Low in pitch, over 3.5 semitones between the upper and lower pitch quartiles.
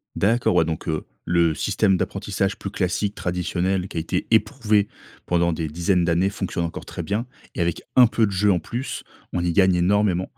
No: very low, 95 Hz; average, 3.0 semitones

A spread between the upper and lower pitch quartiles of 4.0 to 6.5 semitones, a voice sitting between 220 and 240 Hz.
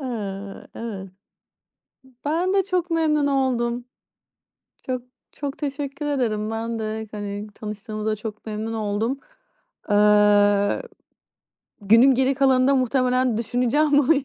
Yes: average, 4.4 semitones; high, 235 Hz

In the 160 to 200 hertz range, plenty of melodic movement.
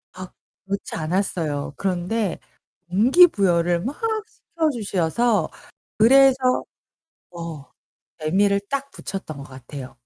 Yes: high, 190 Hz; wide, 6.3 semitones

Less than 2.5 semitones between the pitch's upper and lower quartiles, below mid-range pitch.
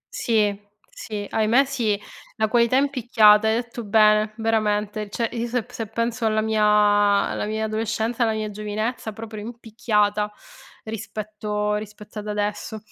No: narrow, 1.4 semitones; high, 215 Hz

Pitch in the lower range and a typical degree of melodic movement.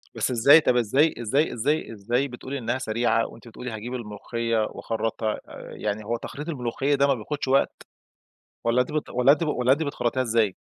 Yes: low, 120 Hz; average, 3.4 semitones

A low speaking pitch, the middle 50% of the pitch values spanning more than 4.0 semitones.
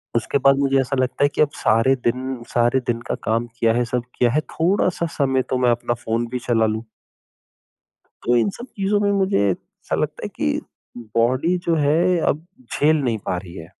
Yes: low, 130 Hz; average, 4.6 semitones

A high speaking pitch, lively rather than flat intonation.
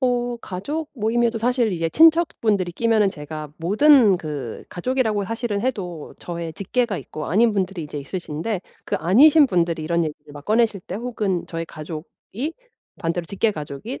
Yes: high, 200 Hz; wide, 6.2 semitones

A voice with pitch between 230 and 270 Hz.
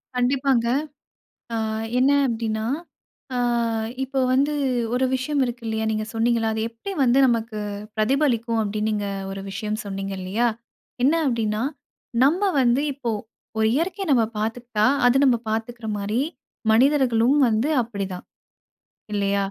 Yes: high, 235 Hz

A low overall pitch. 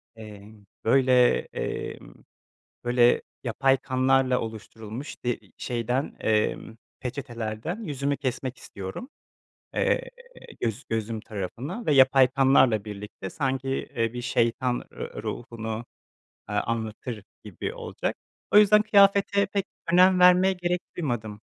Yes: low, 125 Hz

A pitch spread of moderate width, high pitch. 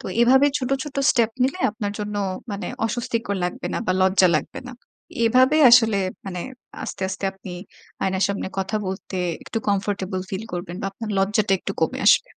Yes: average, 3.6 semitones; high, 205 Hz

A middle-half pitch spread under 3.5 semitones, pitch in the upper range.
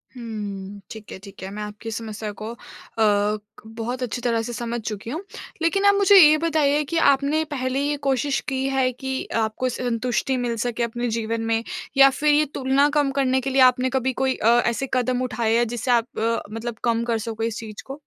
Yes: average, 3.1 semitones; high, 245 Hz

